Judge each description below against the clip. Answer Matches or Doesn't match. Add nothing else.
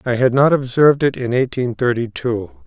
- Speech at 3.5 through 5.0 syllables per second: Doesn't match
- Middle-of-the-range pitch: Doesn't match